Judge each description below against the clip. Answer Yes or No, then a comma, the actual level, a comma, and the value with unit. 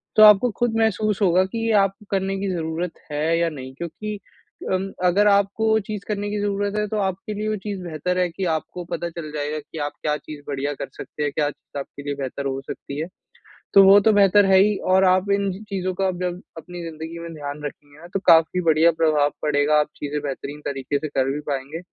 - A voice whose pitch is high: No, medium, 170 Hz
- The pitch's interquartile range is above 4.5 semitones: Yes, average, 5.0 semitones